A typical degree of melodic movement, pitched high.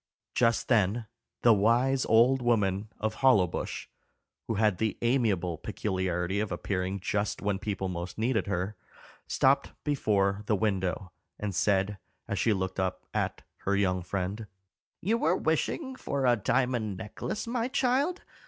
No: average, 4.6 semitones; low, 105 Hz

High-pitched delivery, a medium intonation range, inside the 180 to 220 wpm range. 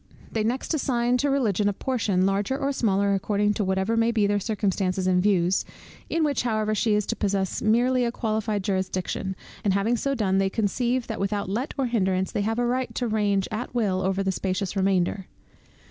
Yes: high, 210 Hz; average, 3.6 semitones; average, 200 wpm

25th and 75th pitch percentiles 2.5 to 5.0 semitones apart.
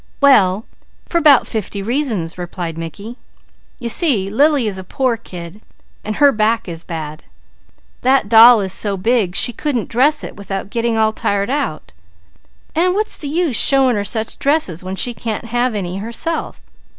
No: wide, 5.4 semitones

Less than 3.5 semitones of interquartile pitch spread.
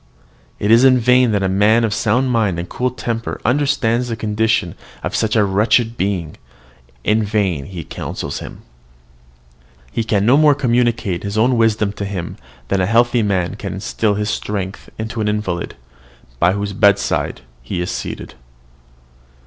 Yes: average, 2.9 semitones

